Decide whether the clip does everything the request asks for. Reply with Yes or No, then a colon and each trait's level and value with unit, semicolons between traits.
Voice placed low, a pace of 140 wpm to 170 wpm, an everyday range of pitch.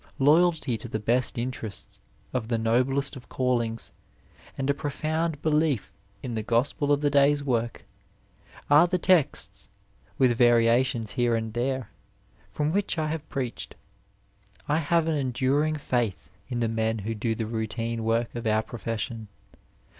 Yes: low, 125 Hz; average, 150 wpm; average, 4.1 semitones